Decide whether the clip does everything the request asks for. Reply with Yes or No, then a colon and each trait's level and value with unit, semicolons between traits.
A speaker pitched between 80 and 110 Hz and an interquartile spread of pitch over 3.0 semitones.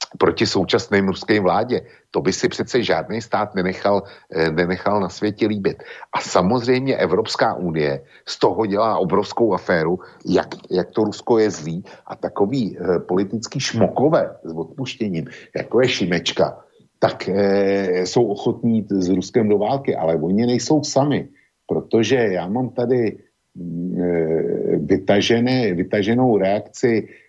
Yes: low, 100 Hz; average, 4.7 semitones